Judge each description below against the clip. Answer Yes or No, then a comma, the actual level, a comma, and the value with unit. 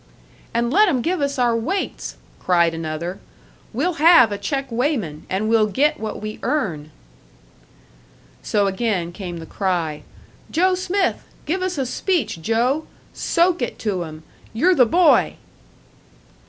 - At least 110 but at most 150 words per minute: Yes, average, 140 wpm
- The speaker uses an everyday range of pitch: No, wide, 8.8 semitones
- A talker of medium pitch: No, high, 235 Hz